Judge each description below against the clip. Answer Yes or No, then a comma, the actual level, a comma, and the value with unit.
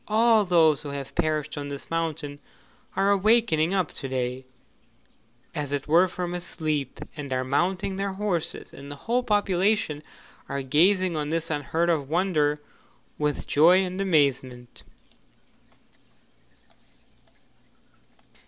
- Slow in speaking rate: Yes, slow, 125 wpm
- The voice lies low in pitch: No, medium, 160 Hz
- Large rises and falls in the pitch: No, average, 4.6 semitones